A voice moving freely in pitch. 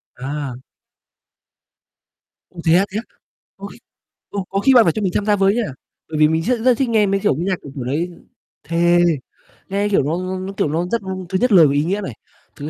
No: average, 4.6 semitones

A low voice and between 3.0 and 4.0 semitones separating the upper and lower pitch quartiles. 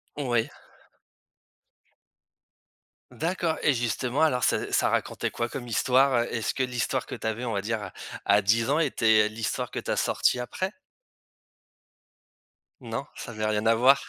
Yes: low, 120 Hz; average, 3.3 semitones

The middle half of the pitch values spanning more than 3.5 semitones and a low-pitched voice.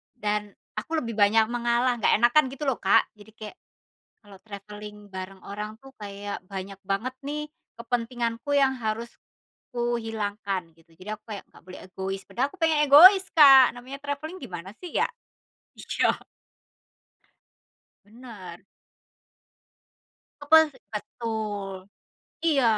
No: average, 4.6 semitones; high, 225 Hz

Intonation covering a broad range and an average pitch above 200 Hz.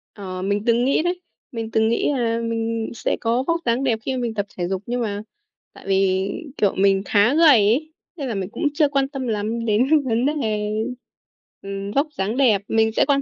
No: average, 4.7 semitones; high, 230 Hz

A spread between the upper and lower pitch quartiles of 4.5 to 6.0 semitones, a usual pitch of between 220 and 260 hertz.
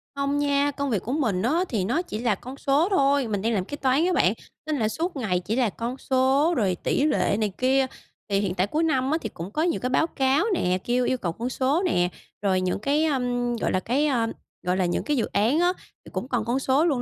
Yes: average, 5.2 semitones; very high, 255 Hz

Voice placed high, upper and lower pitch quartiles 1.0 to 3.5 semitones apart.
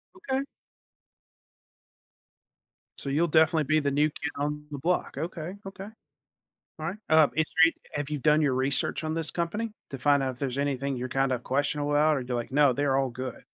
No: medium, 145 Hz; average, 2.7 semitones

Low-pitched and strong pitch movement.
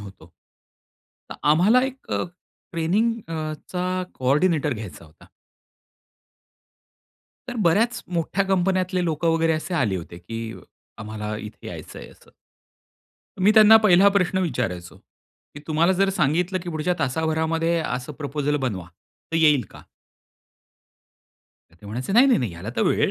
No: medium, 160 Hz; wide, 6.9 semitones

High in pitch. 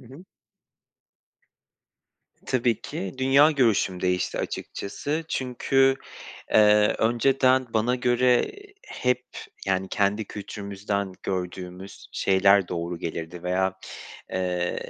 No: low, 105 Hz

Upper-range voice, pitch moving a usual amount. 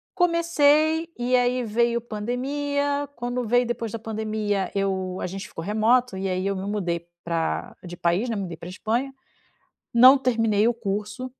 Yes: high, 225 Hz; average, 4.4 semitones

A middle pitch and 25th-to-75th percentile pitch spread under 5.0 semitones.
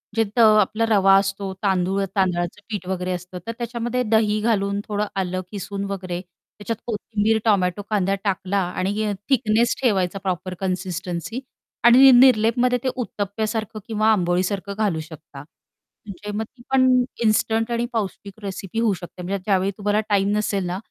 No: high, 200 Hz; average, 2.9 semitones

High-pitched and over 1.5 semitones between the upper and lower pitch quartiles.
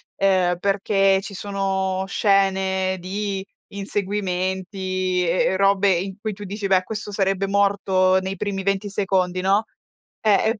No: high, 195 Hz; narrow, 1.2 semitones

